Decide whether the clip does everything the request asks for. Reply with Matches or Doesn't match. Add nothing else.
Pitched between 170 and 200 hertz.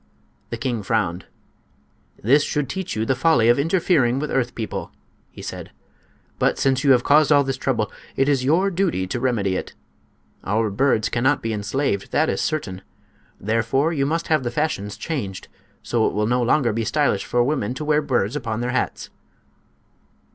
Doesn't match